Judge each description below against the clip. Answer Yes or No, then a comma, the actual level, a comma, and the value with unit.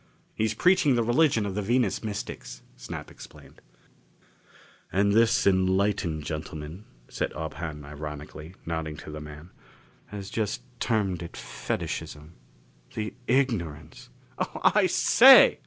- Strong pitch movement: Yes, wide, 6.1 semitones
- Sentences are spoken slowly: Yes, slow, 125 wpm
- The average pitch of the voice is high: No, very low, 95 Hz